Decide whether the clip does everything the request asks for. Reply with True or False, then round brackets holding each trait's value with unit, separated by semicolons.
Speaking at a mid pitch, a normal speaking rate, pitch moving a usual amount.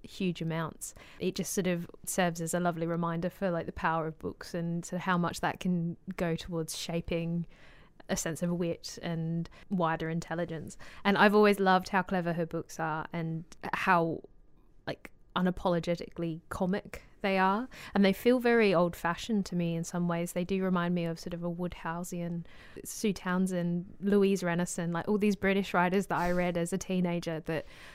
False (175 Hz; 180 wpm; 2.1 semitones)